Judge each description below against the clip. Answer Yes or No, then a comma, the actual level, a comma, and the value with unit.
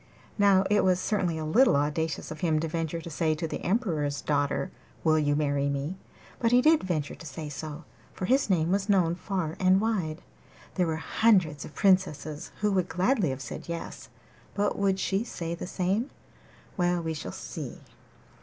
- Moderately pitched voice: Yes, medium, 170 Hz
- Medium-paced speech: Yes, average, 185 wpm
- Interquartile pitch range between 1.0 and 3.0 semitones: No, average, 3.9 semitones